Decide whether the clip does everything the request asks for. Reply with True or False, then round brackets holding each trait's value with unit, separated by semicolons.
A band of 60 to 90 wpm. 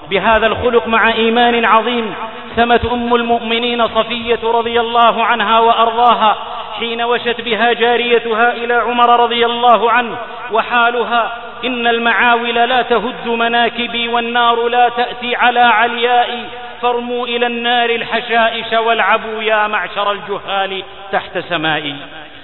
False (115 wpm)